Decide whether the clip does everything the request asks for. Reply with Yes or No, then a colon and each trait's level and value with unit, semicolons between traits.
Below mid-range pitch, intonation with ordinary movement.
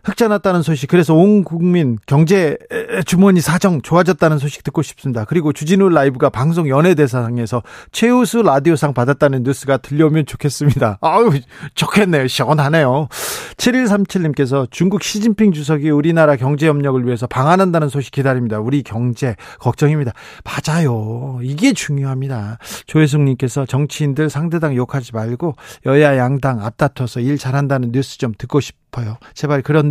No: medium, 145 Hz; average, 4.2 semitones